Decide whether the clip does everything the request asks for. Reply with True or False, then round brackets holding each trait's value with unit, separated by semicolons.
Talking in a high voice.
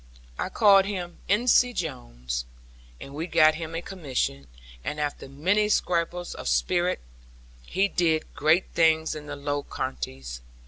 False (160 Hz)